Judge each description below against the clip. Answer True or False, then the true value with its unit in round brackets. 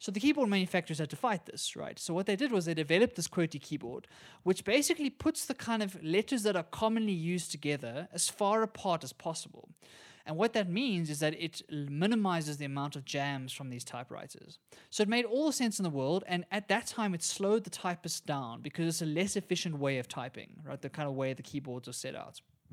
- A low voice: False (175 Hz)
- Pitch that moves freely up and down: True (5.8 semitones)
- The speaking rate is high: True (230 wpm)